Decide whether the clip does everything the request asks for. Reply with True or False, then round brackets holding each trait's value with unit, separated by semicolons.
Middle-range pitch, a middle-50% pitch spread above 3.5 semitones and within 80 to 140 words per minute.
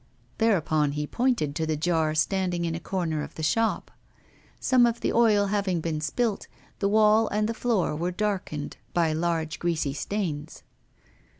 False (175 Hz; 5.2 semitones; 165 wpm)